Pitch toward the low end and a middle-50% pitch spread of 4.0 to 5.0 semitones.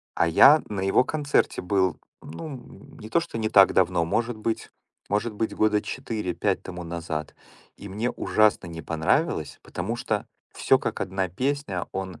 Yes: low, 105 Hz; average, 4.3 semitones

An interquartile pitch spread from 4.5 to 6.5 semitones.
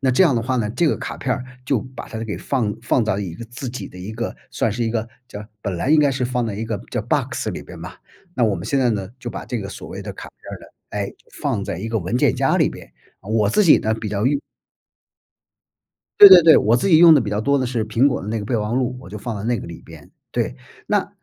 No: average, 3.7 semitones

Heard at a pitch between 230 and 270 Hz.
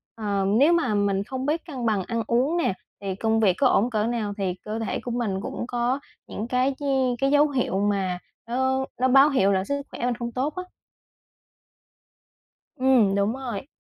Yes: high, 235 Hz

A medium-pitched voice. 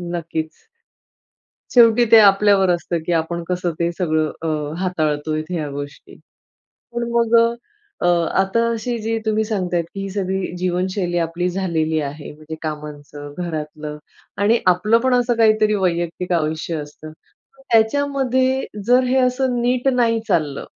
Yes: medium, 180 Hz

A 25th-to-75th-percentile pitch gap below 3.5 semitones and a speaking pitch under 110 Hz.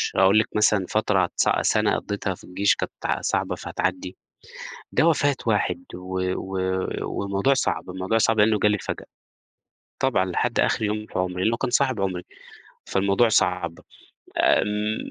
Yes: average, 2.8 semitones; low, 100 Hz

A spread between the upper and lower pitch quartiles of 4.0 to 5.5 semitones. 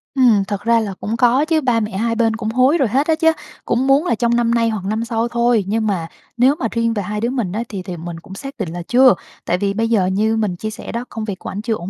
No: average, 3.0 semitones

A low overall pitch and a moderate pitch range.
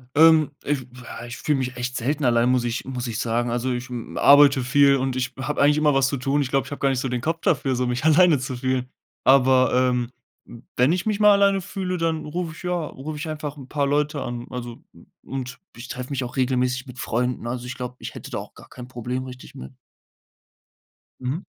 Yes: low, 130 Hz; average, 3.0 semitones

